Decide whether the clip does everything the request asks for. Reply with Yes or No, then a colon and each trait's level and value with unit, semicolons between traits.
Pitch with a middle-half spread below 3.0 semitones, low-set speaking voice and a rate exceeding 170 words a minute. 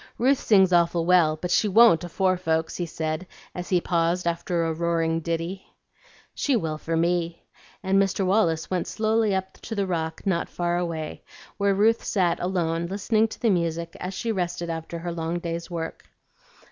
No: narrow, 2.5 semitones; medium, 175 Hz; average, 180 wpm